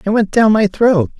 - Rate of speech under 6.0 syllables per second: Yes, 5.0 syllables/s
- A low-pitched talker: No, high, 205 Hz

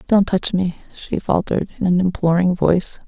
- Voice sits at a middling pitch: Yes, medium, 180 Hz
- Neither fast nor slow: Yes, average, 175 wpm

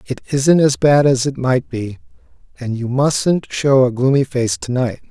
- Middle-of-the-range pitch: No, low, 130 Hz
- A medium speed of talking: No, fast, 225 wpm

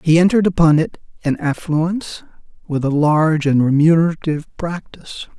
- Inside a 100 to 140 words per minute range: Yes, slow, 135 wpm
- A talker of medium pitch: Yes, medium, 160 Hz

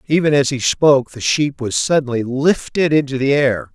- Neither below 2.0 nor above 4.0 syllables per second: No, 5.0 syllables/s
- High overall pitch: No, low, 135 Hz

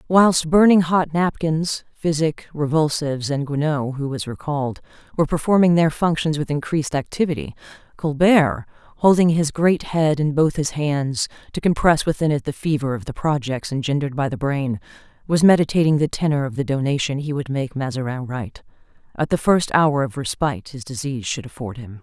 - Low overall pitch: No, medium, 145 Hz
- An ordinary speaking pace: Yes, average, 170 wpm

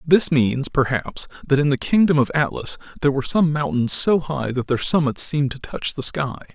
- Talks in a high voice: No, medium, 140 Hz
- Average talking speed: No, fast, 210 wpm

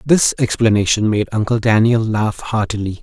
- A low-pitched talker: Yes, low, 110 Hz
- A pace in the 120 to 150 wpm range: Yes, average, 140 wpm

